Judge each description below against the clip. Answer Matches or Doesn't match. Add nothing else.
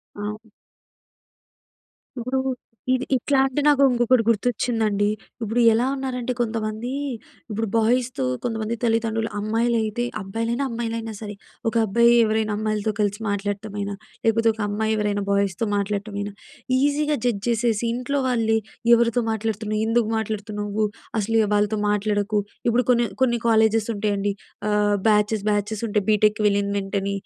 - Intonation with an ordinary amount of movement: Doesn't match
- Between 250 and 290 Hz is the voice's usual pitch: Doesn't match